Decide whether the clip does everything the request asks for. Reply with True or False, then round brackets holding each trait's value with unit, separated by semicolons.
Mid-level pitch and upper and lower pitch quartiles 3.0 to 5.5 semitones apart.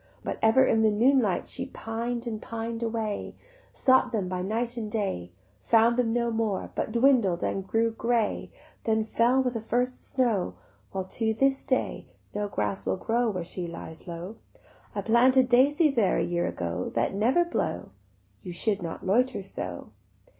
False (225 Hz; 3.8 semitones)